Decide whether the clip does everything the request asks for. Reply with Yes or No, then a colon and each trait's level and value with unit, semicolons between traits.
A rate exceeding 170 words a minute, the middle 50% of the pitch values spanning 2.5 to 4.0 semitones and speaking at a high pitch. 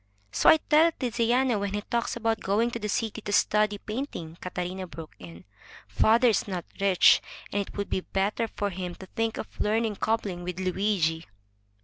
Yes: average, 185 wpm; average, 3.7 semitones; high, 205 Hz